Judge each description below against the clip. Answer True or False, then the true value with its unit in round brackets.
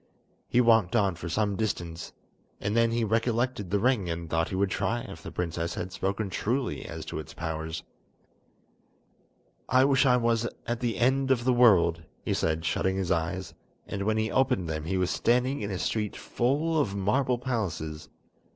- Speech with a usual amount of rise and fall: False (5.7 semitones)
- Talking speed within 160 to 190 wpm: True (185 wpm)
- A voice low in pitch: True (105 Hz)